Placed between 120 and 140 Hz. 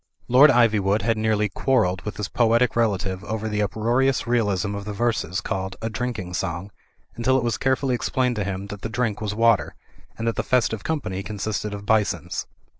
No: low, 110 Hz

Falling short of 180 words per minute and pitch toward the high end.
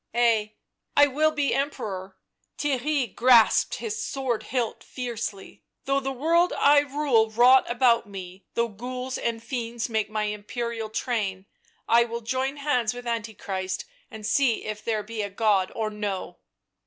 Yes: average, 170 wpm; high, 235 Hz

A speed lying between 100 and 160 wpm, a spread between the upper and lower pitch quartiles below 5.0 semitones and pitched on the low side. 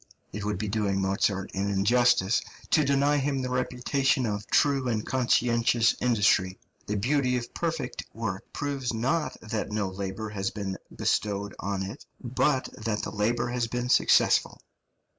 Yes: average, 155 wpm; average, 3.9 semitones; low, 115 Hz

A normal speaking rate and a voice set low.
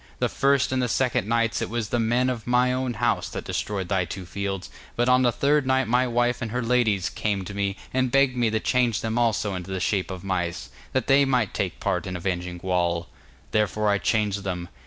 No: fast, 225 wpm; low, 110 Hz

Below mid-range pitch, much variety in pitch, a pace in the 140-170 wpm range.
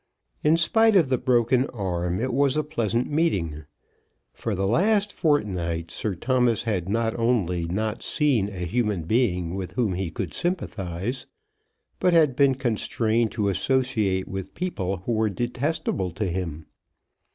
Yes: low, 110 Hz; wide, 5.9 semitones; average, 150 wpm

